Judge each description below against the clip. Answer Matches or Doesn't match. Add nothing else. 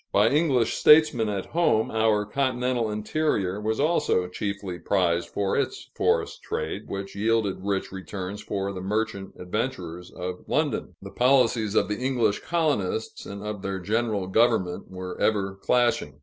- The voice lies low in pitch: Matches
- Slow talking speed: Doesn't match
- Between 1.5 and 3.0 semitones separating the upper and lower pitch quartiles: Doesn't match